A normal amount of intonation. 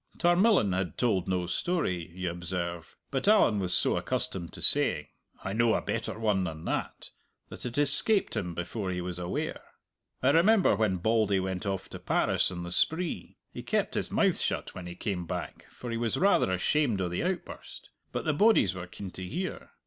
No: wide, 7.8 semitones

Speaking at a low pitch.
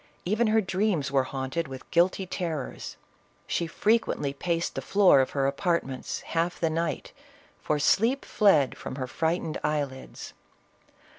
No: medium, 165 Hz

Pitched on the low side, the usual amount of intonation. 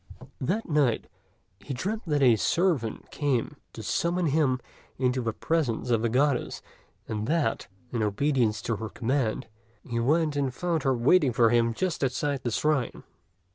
Yes: low, 130 Hz; average, 4.5 semitones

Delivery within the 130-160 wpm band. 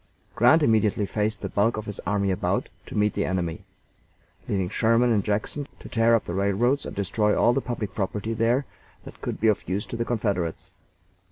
No: average, 195 wpm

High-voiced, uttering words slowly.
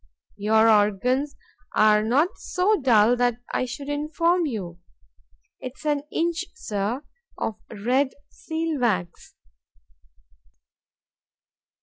Yes: high, 245 Hz; slow, 90 wpm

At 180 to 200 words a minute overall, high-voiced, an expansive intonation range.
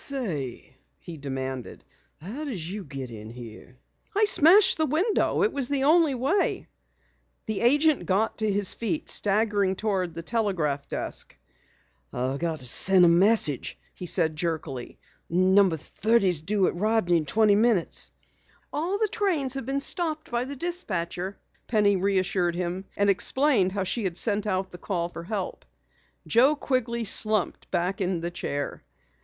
No: average, 155 wpm; high, 200 Hz; wide, 6.4 semitones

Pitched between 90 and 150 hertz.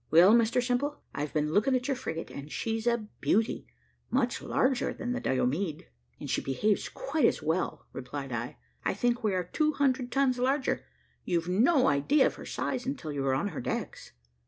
No: high, 225 Hz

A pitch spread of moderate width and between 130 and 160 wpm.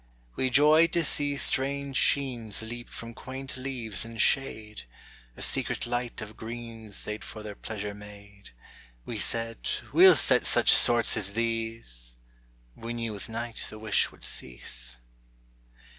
Yes: average, 3.5 semitones; average, 145 wpm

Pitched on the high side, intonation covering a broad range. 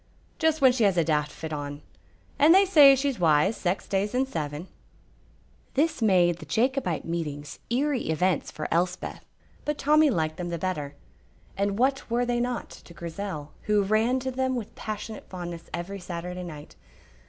Yes: high, 195 Hz; wide, 7.2 semitones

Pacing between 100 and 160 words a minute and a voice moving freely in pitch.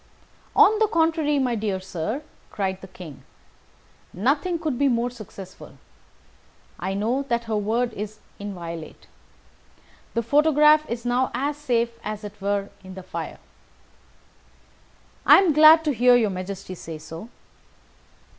Yes: average, 140 wpm; wide, 6.6 semitones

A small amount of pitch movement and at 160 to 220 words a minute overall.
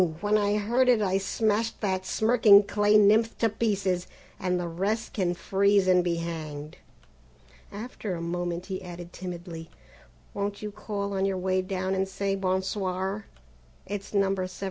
Yes: narrow, 2.2 semitones; average, 165 wpm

